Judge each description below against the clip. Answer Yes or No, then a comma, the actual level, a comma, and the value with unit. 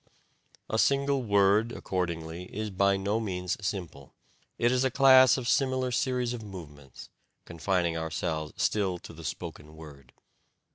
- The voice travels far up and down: Yes, wide, 6.5 semitones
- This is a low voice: Yes, very low, 95 Hz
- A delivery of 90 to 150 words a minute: Yes, average, 140 wpm